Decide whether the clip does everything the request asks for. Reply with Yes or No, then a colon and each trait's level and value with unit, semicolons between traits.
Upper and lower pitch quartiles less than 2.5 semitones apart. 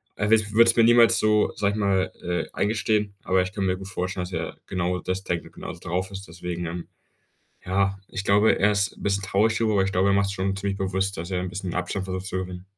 Yes: narrow, 1.8 semitones